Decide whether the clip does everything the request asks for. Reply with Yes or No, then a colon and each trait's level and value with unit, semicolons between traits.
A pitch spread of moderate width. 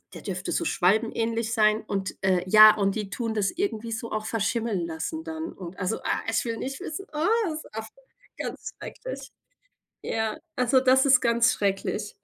Yes: average, 3.7 semitones